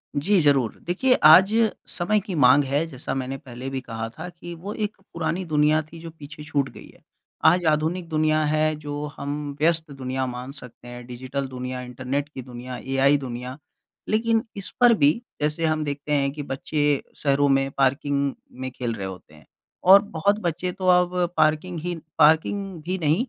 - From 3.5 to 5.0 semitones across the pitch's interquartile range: Yes, average, 4.3 semitones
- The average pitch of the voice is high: No, medium, 150 Hz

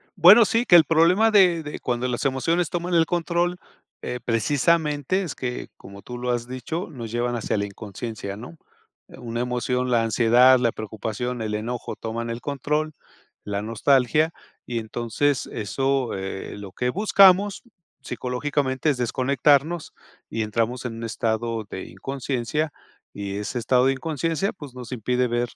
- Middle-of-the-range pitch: No, low, 125 Hz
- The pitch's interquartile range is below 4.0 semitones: No, average, 4.9 semitones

